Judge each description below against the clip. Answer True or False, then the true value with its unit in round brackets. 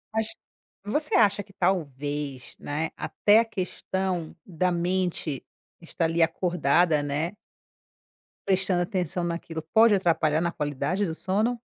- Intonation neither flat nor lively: True (3.5 semitones)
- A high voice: False (175 Hz)